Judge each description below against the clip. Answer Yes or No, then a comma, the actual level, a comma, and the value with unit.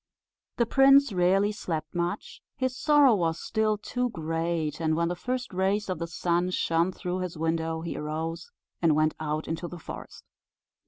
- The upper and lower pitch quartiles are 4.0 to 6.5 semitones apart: Yes, average, 4.3 semitones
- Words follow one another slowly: No, average, 170 wpm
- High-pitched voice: No, medium, 175 Hz